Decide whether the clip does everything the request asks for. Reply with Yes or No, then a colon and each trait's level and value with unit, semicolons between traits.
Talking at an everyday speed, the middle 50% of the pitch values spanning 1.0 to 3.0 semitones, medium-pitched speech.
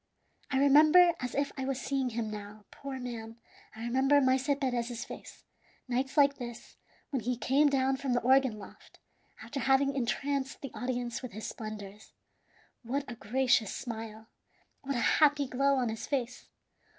No: average, 165 wpm; average, 2.7 semitones; very high, 255 Hz